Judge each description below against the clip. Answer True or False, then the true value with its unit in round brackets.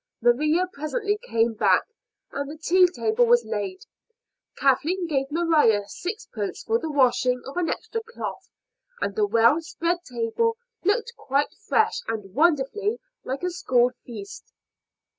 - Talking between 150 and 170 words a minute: False (140 wpm)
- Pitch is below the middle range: False (320 Hz)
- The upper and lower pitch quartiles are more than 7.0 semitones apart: True (8.2 semitones)